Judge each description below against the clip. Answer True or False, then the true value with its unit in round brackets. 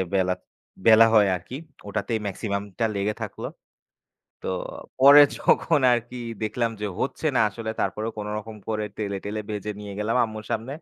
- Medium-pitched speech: False (110 Hz)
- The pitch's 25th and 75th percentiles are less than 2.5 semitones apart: True (2.0 semitones)